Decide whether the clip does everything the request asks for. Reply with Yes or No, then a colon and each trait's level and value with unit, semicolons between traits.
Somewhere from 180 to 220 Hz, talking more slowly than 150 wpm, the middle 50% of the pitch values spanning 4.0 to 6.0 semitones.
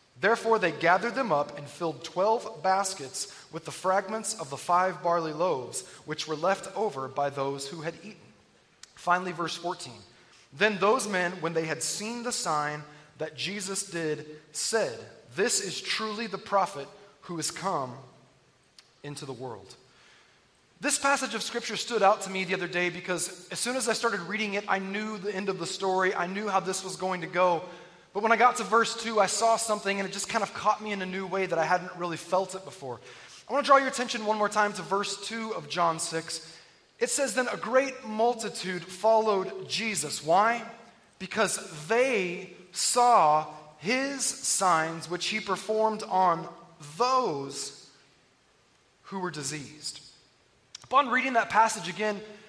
No: high, 190 Hz; average, 180 wpm; average, 4.7 semitones